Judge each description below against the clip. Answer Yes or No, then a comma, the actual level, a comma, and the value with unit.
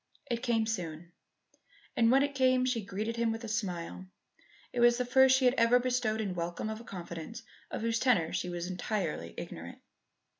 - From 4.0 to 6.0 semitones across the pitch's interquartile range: Yes, average, 5.3 semitones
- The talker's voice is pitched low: No, high, 225 Hz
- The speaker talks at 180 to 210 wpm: Yes, average, 190 wpm